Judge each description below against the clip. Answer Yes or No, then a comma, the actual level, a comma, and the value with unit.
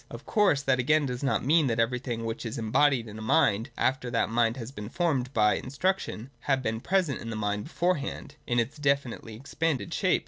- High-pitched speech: No, low, 125 Hz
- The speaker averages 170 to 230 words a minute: Yes, fast, 205 wpm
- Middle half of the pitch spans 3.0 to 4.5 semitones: Yes, average, 4.0 semitones